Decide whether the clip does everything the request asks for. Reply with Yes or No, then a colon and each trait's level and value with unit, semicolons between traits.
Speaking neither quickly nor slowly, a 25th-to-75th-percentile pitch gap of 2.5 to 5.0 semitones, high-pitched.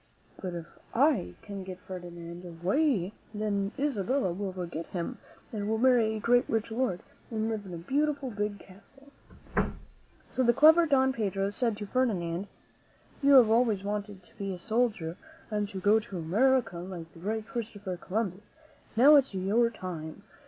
Yes: average, 160 wpm; average, 4.6 semitones; high, 210 Hz